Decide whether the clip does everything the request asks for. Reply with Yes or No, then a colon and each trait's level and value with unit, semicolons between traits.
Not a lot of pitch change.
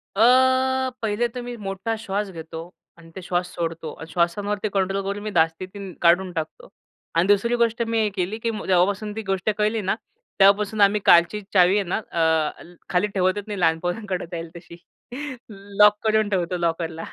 No: average, 3.3 semitones